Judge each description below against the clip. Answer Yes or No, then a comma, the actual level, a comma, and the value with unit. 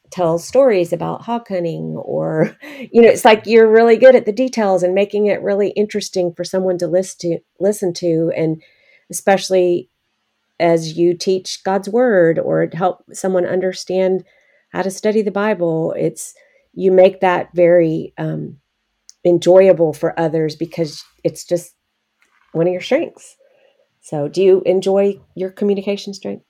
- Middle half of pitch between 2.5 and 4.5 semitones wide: Yes, average, 3.2 semitones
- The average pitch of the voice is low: No, medium, 185 Hz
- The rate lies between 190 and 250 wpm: No, average, 150 wpm